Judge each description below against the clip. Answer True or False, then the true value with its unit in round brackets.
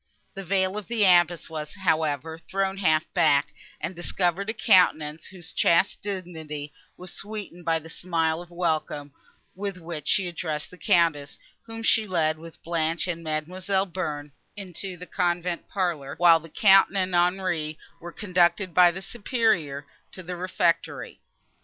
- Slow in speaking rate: False (155 wpm)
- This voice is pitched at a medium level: True (175 Hz)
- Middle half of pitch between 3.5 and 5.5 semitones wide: False (2.8 semitones)